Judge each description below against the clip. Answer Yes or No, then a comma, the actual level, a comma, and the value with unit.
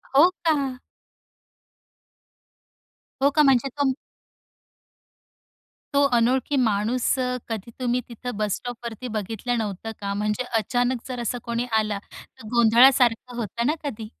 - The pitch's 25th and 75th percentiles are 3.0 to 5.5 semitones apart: No, narrow, 2.5 semitones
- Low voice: No, high, 240 Hz